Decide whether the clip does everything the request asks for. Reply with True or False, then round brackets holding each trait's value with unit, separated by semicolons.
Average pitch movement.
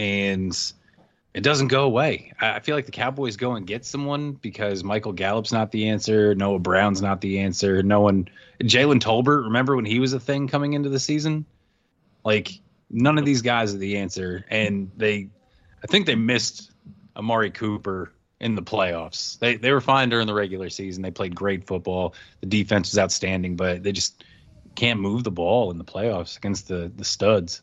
True (4.2 semitones)